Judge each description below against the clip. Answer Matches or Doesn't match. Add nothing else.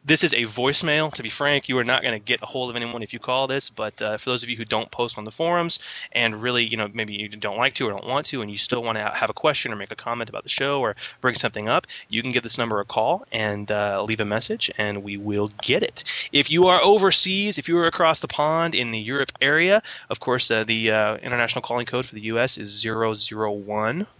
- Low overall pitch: Matches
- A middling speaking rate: Doesn't match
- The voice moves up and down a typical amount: Matches